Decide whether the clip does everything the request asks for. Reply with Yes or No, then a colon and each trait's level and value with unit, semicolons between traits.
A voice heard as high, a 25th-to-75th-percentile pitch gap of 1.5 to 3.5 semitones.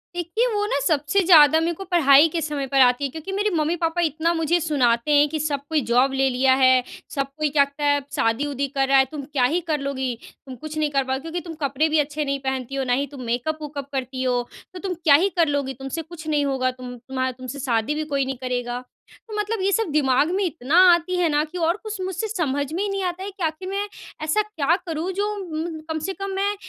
No: very high, 295 Hz; average, 4.2 semitones